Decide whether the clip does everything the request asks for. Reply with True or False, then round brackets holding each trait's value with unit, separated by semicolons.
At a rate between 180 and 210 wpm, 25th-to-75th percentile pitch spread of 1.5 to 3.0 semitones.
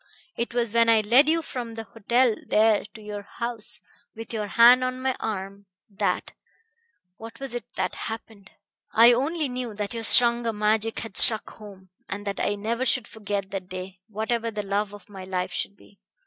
True (190 wpm; 2.7 semitones)